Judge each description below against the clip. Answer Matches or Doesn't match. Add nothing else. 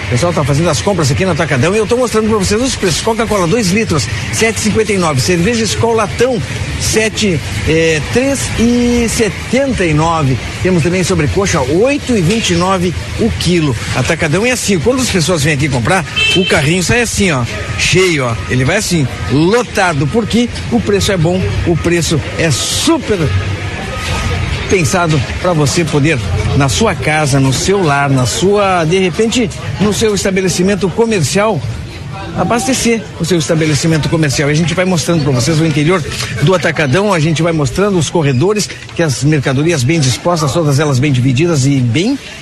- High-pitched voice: Doesn't match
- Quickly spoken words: Doesn't match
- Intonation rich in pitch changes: Matches